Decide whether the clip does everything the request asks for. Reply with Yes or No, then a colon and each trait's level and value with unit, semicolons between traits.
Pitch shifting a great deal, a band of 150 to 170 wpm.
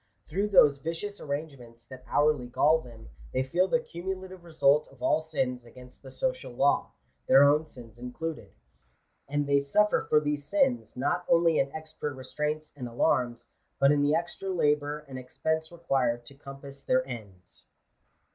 No: average, 4.0 semitones; average, 165 wpm